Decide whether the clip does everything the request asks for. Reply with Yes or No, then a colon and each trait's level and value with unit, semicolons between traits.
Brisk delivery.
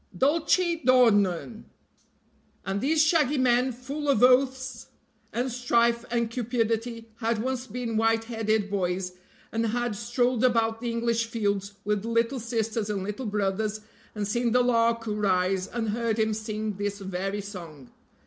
No: average, 145 wpm